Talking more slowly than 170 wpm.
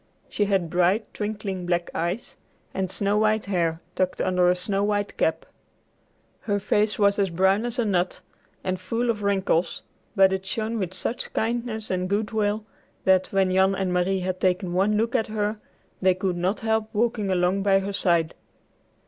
No: average, 180 wpm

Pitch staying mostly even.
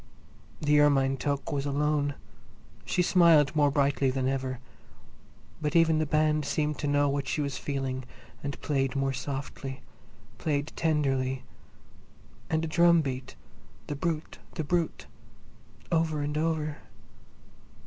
Yes: narrow, 2.2 semitones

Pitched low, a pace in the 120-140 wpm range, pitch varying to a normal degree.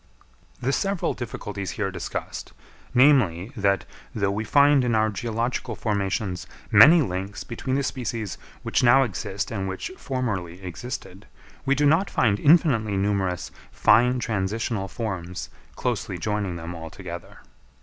Yes: low, 110 Hz; slow, 135 wpm; average, 4.6 semitones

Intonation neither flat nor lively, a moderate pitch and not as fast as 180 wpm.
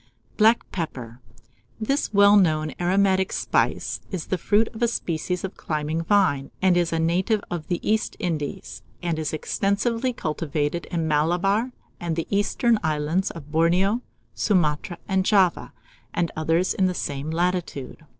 Yes: average, 4.1 semitones; medium, 175 Hz; average, 150 wpm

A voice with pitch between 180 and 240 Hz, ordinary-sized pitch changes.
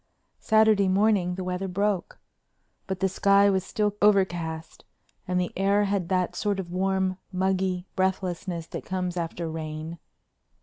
No: medium, 185 Hz; narrow, 1.9 semitones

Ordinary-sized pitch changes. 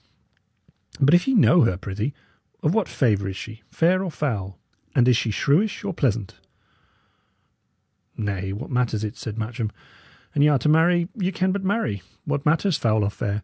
No: wide, 8.4 semitones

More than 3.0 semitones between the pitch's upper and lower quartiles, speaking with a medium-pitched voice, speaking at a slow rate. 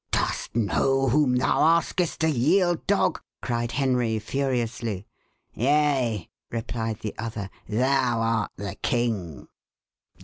No: average, 3.4 semitones; low, 120 Hz; slow, 110 wpm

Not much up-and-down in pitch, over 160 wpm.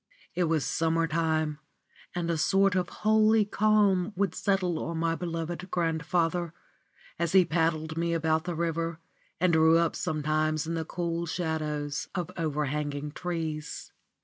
No: narrow, 2.0 semitones; average, 145 wpm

